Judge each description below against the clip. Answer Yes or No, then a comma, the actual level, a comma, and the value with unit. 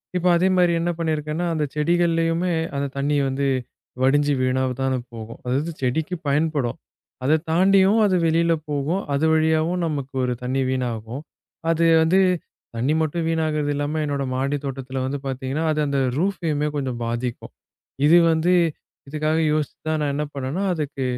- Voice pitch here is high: No, medium, 150 Hz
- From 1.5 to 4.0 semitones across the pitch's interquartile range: Yes, average, 3.5 semitones